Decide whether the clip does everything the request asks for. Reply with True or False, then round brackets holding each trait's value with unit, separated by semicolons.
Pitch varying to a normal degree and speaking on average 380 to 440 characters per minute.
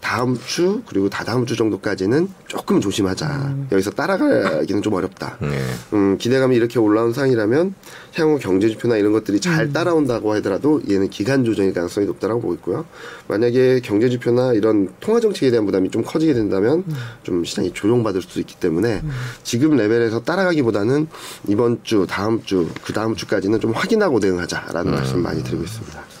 False (6.3 semitones; 415 characters per minute)